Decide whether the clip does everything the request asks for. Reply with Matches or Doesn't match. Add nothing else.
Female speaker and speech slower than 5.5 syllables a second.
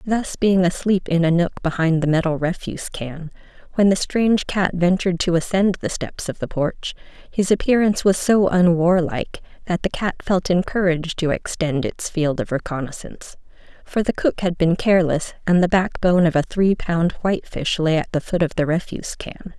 Matches